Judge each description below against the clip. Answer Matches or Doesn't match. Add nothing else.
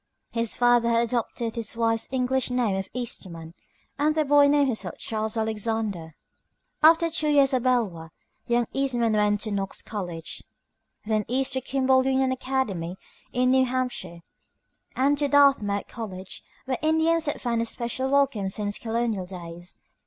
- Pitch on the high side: Matches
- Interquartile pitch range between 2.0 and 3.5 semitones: Doesn't match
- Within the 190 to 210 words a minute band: Doesn't match